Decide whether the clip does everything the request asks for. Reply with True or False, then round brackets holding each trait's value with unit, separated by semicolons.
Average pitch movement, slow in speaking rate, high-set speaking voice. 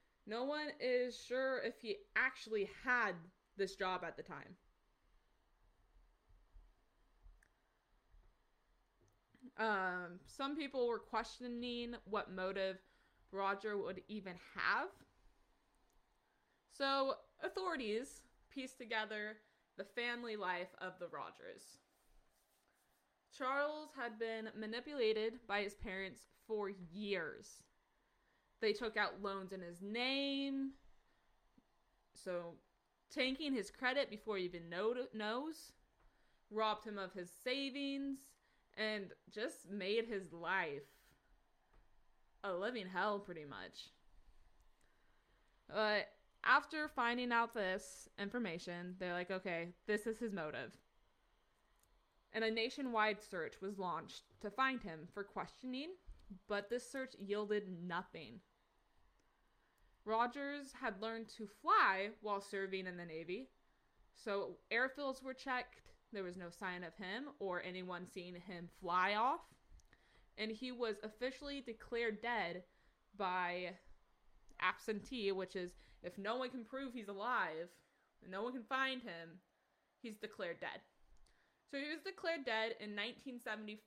True (4.7 semitones; 115 wpm; 215 Hz)